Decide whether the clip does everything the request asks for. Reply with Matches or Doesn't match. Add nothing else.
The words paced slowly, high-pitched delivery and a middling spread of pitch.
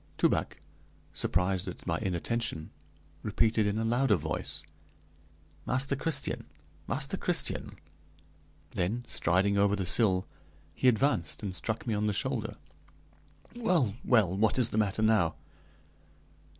Doesn't match